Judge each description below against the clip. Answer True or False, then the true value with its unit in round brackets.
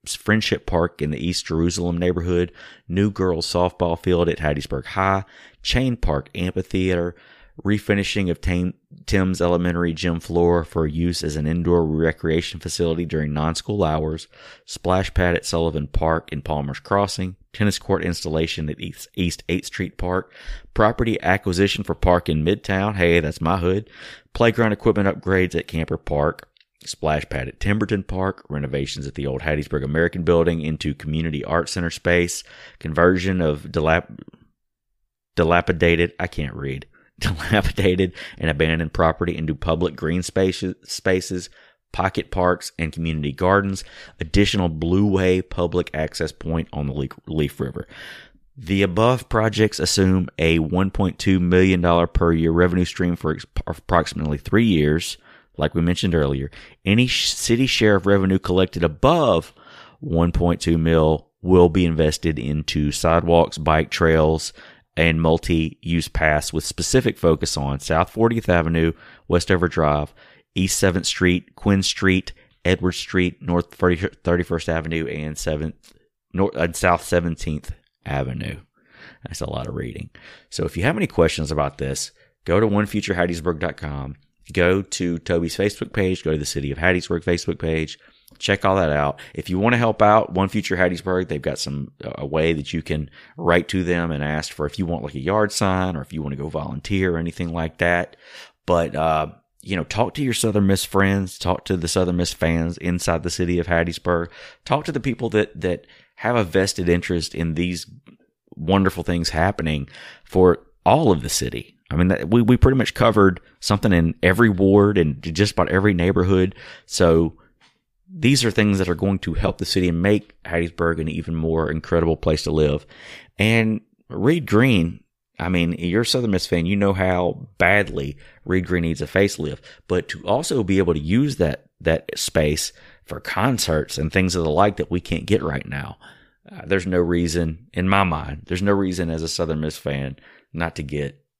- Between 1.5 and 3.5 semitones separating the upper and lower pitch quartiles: True (3.1 semitones)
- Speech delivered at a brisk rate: False (165 wpm)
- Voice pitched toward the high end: False (85 Hz)